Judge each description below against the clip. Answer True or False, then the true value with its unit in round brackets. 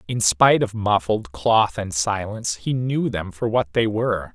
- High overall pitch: False (105 Hz)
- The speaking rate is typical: True (195 wpm)